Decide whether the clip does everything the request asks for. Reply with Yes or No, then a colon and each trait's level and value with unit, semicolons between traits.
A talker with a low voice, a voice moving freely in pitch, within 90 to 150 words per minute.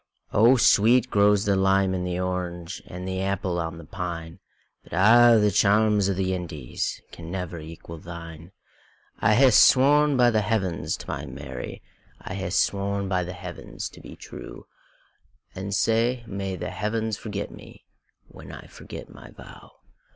No: very low, 95 Hz; average, 3.3 semitones; average, 145 wpm